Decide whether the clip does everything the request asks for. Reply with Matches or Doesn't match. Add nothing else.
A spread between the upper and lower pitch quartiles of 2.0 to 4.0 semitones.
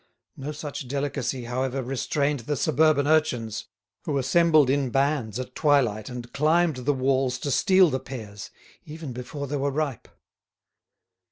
Matches